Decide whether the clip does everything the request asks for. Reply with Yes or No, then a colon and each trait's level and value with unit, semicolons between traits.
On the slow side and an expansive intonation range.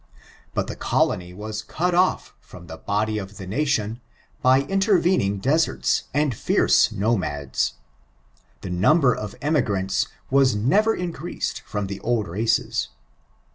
Yes: slow, 130 wpm; wide, 7.4 semitones